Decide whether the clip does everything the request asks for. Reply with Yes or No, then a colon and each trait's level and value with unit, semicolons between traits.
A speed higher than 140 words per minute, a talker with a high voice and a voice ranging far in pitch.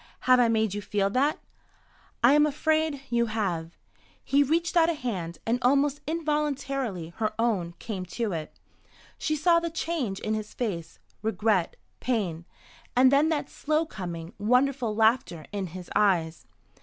Yes: average, 155 wpm; high, 230 Hz; wide, 6.8 semitones